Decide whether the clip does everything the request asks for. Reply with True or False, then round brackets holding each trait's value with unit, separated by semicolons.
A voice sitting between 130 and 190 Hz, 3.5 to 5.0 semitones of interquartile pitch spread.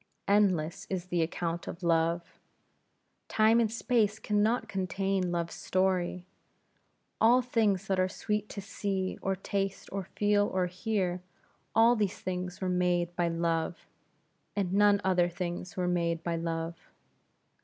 False (185 Hz; 2.9 semitones)